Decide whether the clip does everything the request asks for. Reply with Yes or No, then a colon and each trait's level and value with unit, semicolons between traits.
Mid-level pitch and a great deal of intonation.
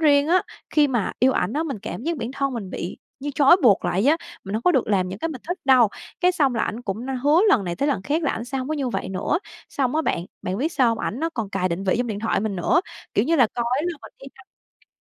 No: very high, 255 Hz; wide, 5.7 semitones